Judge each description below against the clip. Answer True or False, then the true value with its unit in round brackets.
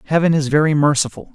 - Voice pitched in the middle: True (150 Hz)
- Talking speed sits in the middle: True (180 wpm)